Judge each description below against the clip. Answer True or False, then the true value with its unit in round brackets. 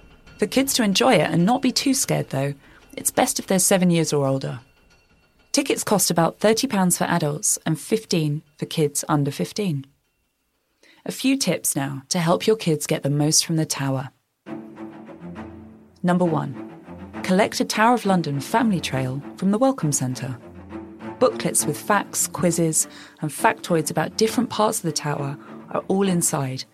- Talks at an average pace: True (165 wpm)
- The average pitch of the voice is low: False (160 Hz)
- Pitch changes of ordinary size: False (7.0 semitones)